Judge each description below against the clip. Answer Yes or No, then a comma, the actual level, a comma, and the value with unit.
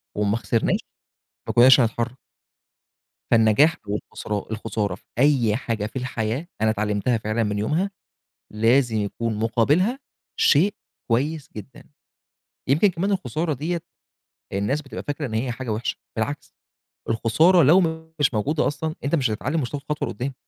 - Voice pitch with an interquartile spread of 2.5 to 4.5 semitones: No, average, 5.3 semitones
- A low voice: Yes, low, 125 Hz